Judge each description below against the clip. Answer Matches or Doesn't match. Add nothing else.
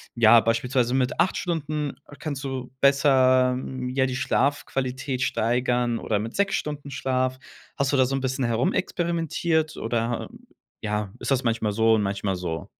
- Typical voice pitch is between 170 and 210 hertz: Doesn't match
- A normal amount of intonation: Matches